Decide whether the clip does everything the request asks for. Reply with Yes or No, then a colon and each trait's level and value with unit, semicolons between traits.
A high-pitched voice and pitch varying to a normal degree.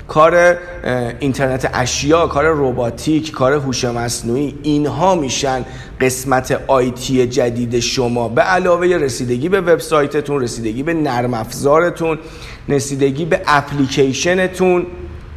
No: medium, 140 Hz; average, 4.3 semitones